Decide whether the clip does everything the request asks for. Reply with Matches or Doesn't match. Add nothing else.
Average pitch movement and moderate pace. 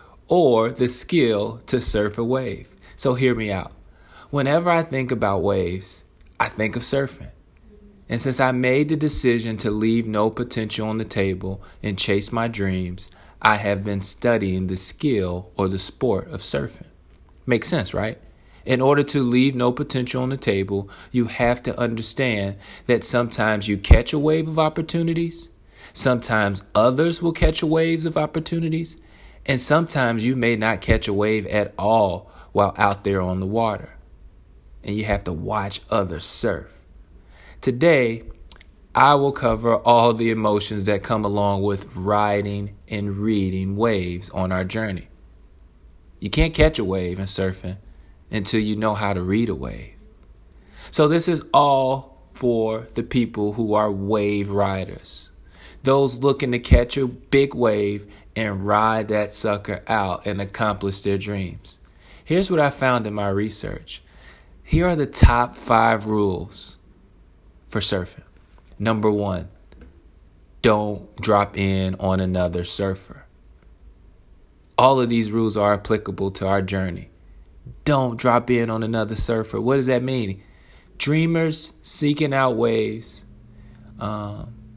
Matches